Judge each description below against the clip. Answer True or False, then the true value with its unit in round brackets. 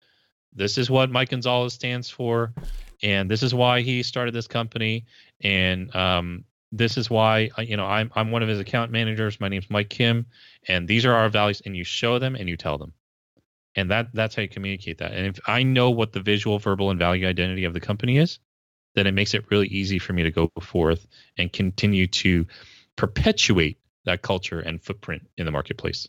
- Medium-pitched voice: False (105 Hz)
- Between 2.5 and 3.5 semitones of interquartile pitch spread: False (4.0 semitones)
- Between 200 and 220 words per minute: True (205 wpm)